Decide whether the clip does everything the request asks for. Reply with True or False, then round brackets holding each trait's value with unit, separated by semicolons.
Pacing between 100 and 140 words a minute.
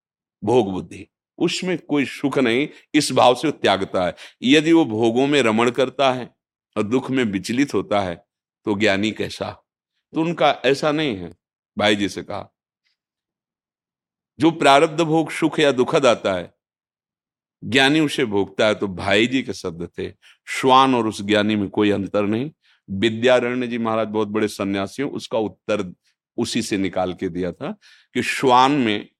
False (160 wpm)